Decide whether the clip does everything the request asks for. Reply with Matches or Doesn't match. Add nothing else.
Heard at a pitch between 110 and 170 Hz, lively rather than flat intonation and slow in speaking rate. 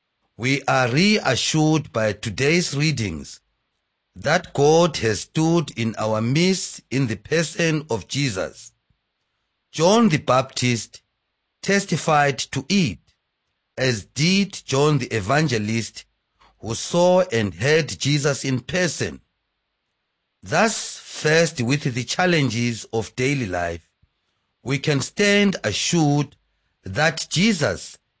Matches